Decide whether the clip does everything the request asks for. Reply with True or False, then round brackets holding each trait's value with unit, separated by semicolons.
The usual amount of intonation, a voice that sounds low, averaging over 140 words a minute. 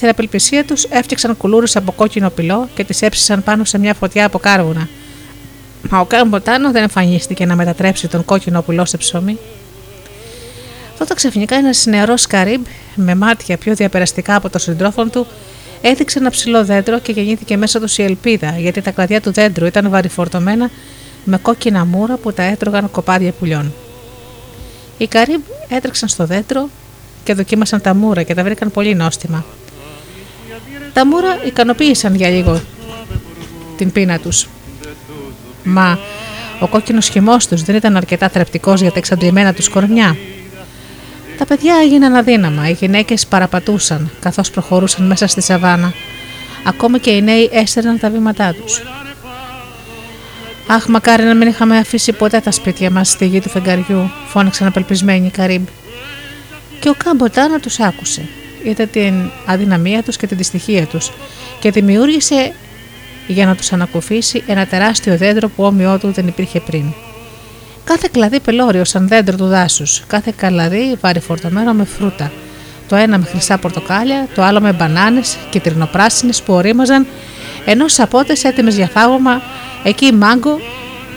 False (4.5 semitones; 195 Hz; 150 wpm)